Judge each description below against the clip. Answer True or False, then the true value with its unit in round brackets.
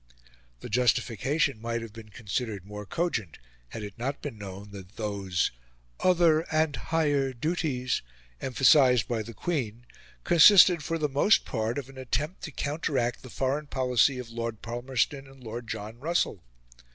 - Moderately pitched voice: False (125 Hz)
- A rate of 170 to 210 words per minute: False (150 wpm)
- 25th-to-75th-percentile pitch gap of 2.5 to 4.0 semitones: False (4.7 semitones)